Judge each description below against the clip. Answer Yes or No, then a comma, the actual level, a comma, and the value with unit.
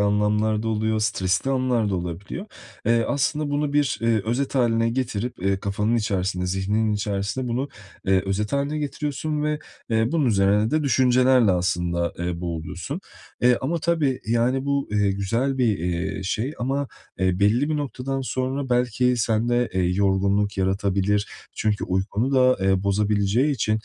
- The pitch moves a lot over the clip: No, average, 5.0 semitones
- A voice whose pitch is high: No, low, 110 Hz